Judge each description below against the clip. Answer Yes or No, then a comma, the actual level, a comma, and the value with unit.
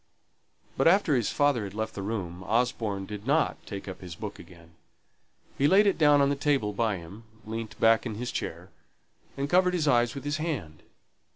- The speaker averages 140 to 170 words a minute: No, average, 195 wpm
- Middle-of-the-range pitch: No, low, 115 Hz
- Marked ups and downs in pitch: Yes, wide, 6.1 semitones